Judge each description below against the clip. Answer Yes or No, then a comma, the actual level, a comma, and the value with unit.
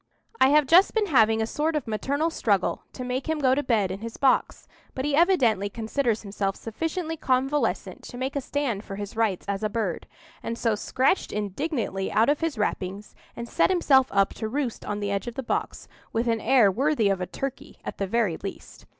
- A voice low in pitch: No, high, 235 Hz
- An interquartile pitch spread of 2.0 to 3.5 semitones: No, wide, 5.5 semitones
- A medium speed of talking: No, fast, 210 wpm